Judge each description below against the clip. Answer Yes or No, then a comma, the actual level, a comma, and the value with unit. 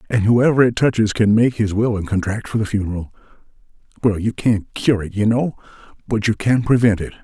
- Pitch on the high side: No, low, 110 Hz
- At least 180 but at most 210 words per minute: Yes, fast, 205 wpm